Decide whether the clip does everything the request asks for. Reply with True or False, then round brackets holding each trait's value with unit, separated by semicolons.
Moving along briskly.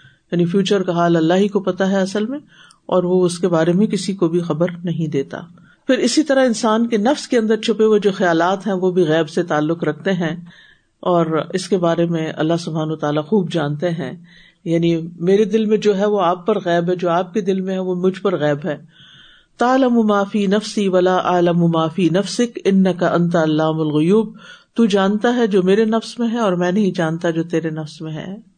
True (220 wpm)